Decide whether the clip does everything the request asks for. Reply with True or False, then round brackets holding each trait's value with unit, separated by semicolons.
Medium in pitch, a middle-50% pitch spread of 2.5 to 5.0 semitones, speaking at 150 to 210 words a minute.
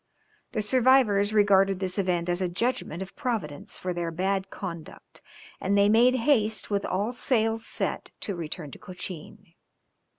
False (200 Hz; 3.5 semitones; 155 wpm)